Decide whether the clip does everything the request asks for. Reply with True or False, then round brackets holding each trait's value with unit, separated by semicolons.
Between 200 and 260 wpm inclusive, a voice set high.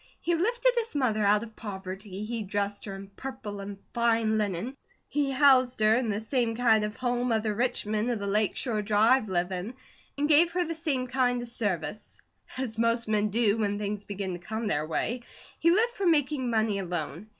True (205 wpm; 220 Hz)